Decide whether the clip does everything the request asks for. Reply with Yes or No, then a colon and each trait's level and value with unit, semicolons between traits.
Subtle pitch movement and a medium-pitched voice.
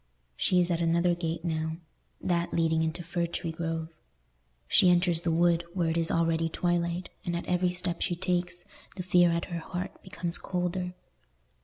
Yes: narrow, 1.2 semitones; medium, 170 Hz